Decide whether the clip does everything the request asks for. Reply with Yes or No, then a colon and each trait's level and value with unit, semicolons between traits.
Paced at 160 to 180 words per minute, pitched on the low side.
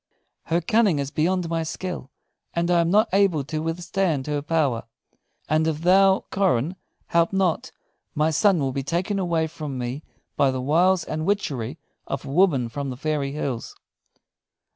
No: average, 165 wpm; medium, 160 Hz